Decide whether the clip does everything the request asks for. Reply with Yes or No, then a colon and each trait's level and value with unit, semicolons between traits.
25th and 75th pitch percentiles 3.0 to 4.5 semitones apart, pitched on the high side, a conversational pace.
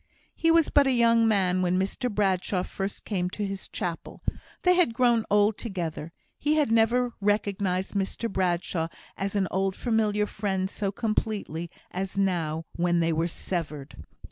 Yes: average, 3.7 semitones; high, 195 Hz; average, 160 wpm